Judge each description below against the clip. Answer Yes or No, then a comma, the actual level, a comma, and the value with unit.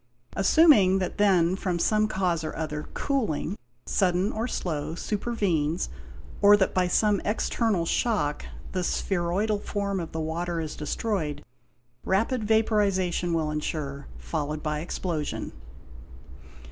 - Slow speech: Yes, slow, 115 wpm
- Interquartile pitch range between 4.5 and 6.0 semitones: Yes, average, 4.8 semitones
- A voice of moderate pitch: Yes, medium, 180 Hz